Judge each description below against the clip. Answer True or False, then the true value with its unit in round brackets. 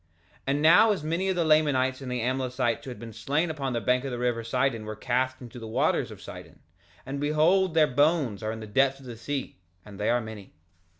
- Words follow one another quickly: True (240 wpm)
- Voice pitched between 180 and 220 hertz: False (130 Hz)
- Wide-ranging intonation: False (4.3 semitones)